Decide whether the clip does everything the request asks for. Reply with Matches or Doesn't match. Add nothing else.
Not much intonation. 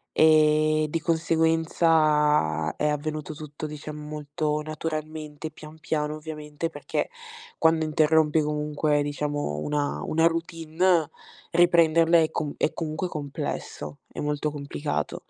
Matches